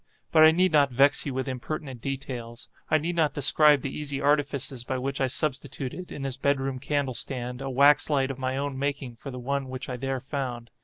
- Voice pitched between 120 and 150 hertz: Yes, low, 135 Hz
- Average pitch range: No, narrow, 1.9 semitones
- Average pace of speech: No, fast, 220 wpm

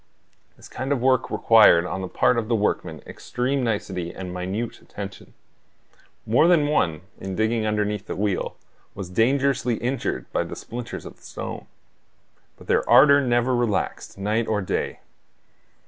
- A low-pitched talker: Yes, low, 110 Hz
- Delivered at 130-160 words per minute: Yes, average, 150 wpm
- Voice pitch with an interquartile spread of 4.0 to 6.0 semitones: Yes, average, 4.3 semitones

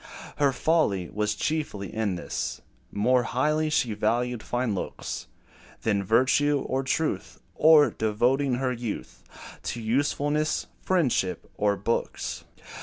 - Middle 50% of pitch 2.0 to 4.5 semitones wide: No, wide, 5.4 semitones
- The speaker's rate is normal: No, slow, 115 wpm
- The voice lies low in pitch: Yes, low, 125 Hz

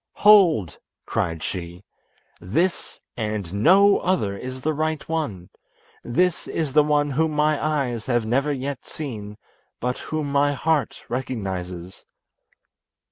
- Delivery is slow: Yes, slow, 125 wpm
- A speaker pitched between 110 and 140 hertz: Yes, low, 135 Hz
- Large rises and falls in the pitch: Yes, wide, 6.8 semitones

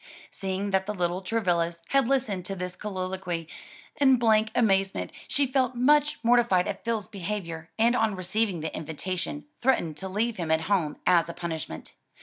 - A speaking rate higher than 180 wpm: No, average, 165 wpm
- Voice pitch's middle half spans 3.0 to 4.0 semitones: No, average, 4.6 semitones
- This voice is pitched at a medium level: No, high, 195 Hz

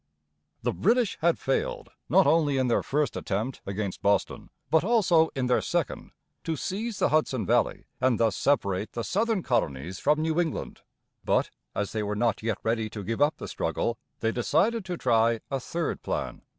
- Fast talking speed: No, average, 180 wpm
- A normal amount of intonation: No, wide, 7.0 semitones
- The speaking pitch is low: Yes, low, 130 Hz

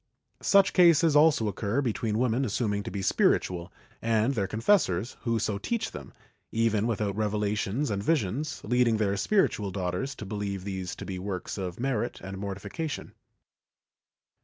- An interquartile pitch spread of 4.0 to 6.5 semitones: Yes, average, 4.6 semitones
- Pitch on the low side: Yes, low, 110 Hz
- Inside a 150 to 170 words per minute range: Yes, average, 155 wpm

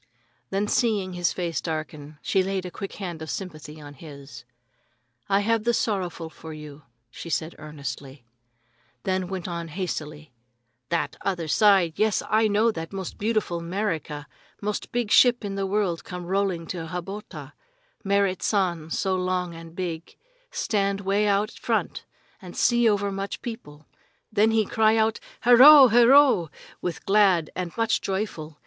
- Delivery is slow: No, average, 155 wpm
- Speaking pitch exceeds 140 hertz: Yes, medium, 185 Hz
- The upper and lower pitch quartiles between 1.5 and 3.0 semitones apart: No, average, 4.2 semitones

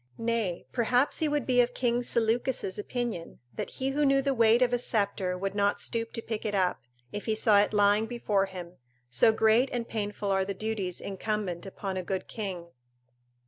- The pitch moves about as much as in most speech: Yes, average, 3.6 semitones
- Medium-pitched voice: No, high, 215 Hz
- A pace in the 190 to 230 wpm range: Yes, average, 195 wpm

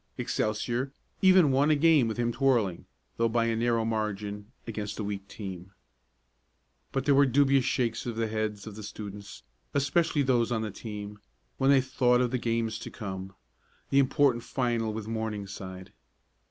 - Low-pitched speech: Yes, low, 115 Hz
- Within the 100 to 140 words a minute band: No, average, 170 wpm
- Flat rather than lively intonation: No, average, 3.8 semitones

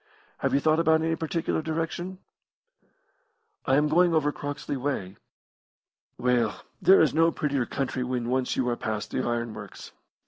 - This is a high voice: No, medium, 145 Hz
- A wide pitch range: No, average, 4.5 semitones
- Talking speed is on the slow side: No, average, 160 wpm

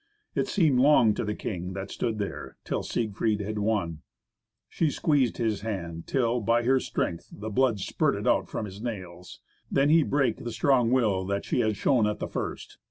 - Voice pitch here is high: No, low, 110 Hz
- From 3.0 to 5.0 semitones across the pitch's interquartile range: Yes, average, 4.1 semitones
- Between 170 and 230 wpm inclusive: Yes, average, 190 wpm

